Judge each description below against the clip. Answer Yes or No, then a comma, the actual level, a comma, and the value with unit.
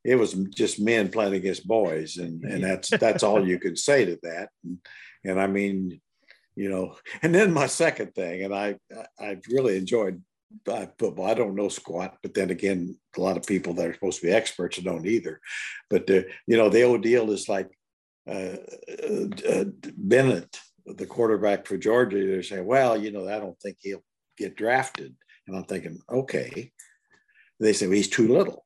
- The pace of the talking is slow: No, average, 195 wpm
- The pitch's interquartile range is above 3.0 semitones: Yes, average, 4.3 semitones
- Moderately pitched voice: No, low, 100 Hz